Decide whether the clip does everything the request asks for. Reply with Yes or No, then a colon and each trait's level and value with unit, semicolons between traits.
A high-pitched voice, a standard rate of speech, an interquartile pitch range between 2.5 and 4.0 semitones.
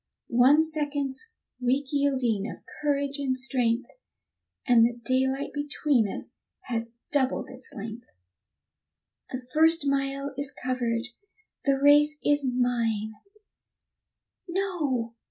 No: very high, 265 Hz; slow, 105 wpm; average, 2.9 semitones